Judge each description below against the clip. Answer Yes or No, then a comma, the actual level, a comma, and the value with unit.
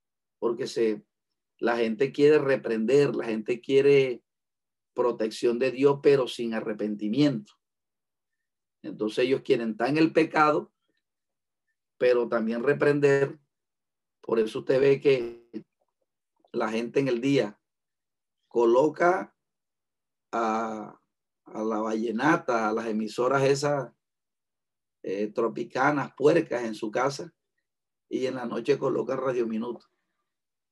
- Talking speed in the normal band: No, slow, 110 wpm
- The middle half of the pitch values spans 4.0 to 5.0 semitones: Yes, average, 4.3 semitones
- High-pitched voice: No, low, 125 Hz